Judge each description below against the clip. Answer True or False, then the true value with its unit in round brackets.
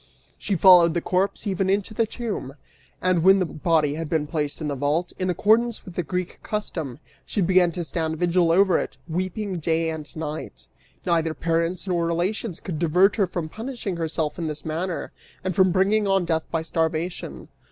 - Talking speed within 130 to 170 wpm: False (185 wpm)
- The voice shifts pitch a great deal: False (2.8 semitones)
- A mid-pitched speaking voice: True (175 Hz)